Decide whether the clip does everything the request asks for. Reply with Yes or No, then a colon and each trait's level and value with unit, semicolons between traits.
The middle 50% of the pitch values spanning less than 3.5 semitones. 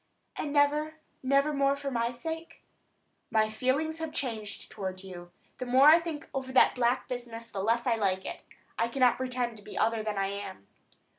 No: average, 4.5 semitones